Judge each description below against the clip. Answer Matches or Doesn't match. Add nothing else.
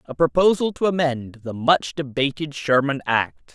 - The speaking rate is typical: Matches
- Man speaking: Matches